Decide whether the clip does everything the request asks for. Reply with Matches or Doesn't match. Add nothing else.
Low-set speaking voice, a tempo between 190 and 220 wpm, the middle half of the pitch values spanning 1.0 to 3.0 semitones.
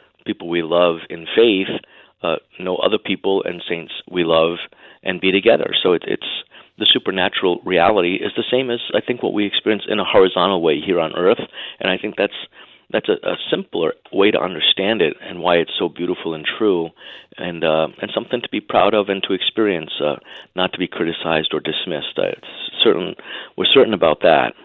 Matches